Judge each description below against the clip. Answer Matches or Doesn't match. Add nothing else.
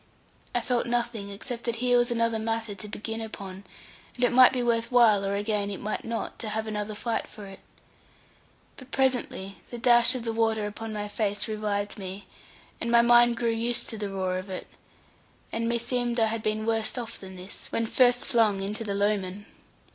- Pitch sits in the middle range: Doesn't match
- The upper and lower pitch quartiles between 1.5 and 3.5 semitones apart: Matches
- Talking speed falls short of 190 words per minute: Doesn't match